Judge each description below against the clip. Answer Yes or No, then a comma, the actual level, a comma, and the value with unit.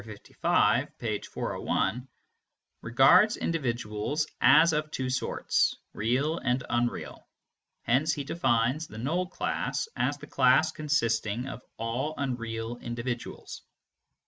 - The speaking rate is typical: No, slow, 110 wpm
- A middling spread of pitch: Yes, average, 4.4 semitones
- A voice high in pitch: No, low, 125 Hz